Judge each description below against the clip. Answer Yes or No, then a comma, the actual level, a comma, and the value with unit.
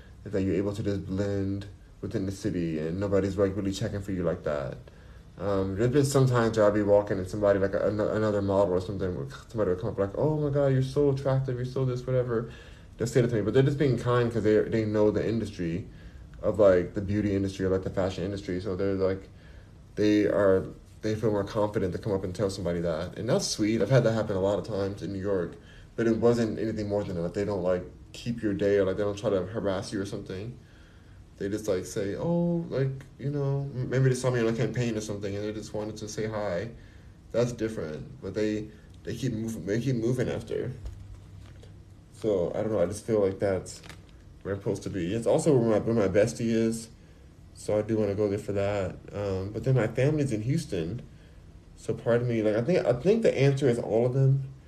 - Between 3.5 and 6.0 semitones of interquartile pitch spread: No, average, 3.1 semitones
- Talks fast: Yes, fast, 240 wpm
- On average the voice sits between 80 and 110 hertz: Yes, low, 105 Hz